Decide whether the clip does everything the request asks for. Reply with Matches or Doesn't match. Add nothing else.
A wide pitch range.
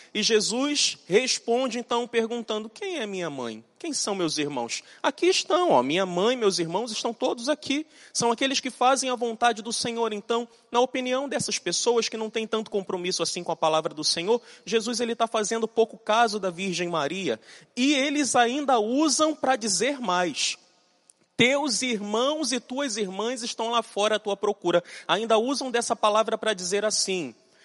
Doesn't match